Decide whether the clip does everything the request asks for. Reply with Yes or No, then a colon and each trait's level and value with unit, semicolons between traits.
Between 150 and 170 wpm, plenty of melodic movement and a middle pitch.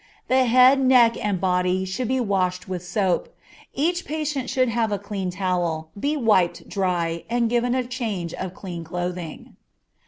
No: average, 160 wpm; wide, 5.7 semitones; high, 200 Hz